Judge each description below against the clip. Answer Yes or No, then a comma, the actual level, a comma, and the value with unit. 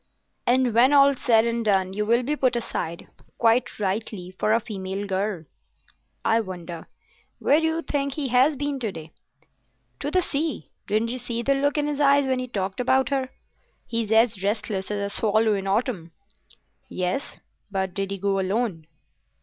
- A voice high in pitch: Yes, high, 225 Hz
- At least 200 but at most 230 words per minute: No, average, 175 wpm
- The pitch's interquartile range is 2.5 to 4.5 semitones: No, average, 5.1 semitones